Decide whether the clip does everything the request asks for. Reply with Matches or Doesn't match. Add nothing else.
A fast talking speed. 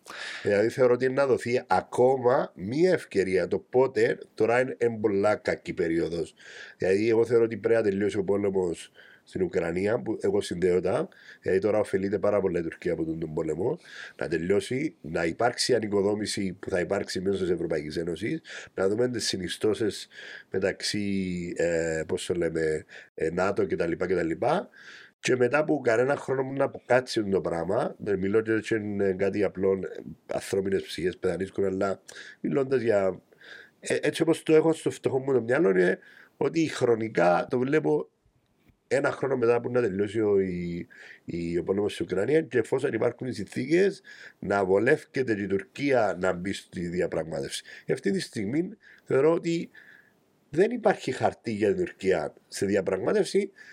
Doesn't match